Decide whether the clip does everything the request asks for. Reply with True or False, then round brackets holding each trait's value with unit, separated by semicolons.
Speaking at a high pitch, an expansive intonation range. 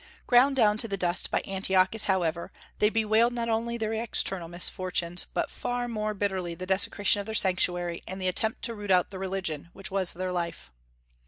False (195 Hz; 3.4 semitones)